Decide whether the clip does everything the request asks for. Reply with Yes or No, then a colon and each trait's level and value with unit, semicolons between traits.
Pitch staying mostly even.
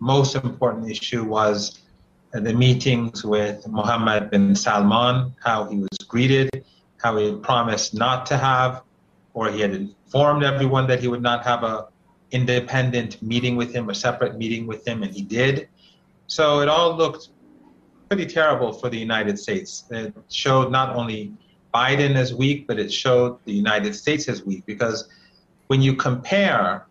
No: average, 3.7 semitones